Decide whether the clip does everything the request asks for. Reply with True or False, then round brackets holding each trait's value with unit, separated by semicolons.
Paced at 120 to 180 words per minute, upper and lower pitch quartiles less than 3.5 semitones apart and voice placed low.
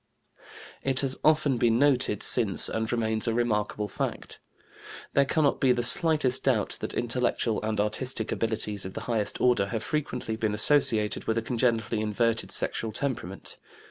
True (160 wpm; 3.1 semitones; 115 Hz)